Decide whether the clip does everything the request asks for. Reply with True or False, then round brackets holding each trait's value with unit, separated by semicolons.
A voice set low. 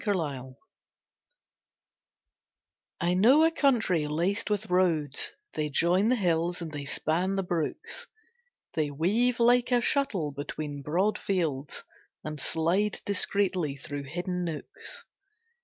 False (175 Hz)